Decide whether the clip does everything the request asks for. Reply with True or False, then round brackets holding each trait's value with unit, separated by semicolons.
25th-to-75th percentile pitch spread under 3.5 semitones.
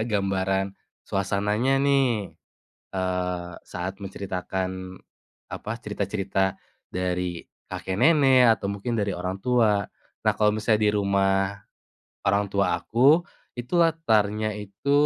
True (2.9 semitones)